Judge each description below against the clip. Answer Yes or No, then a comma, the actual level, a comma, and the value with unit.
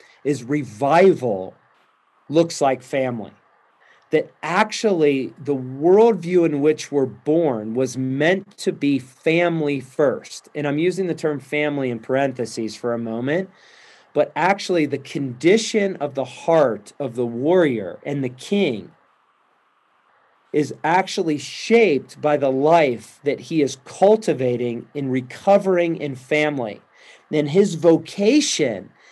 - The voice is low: No, medium, 150 Hz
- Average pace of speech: No, slow, 125 wpm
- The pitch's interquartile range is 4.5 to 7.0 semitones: Yes, average, 5.1 semitones